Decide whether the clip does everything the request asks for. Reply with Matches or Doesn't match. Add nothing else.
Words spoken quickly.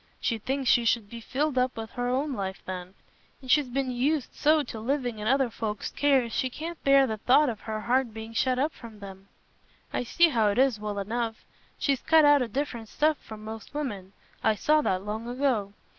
Matches